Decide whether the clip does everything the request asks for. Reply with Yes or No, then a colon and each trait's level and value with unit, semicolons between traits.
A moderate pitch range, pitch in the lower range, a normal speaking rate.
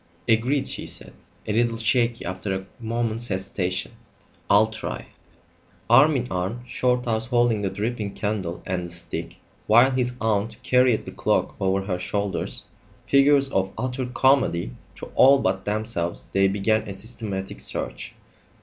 Yes: average, 4.2 semitones; low, 110 Hz; average, 150 wpm